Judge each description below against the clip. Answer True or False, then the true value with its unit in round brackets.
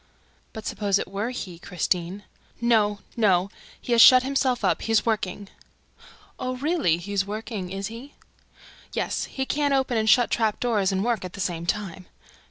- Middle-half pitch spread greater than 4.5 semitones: False (4.1 semitones)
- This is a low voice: False (210 Hz)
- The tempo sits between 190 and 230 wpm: False (180 wpm)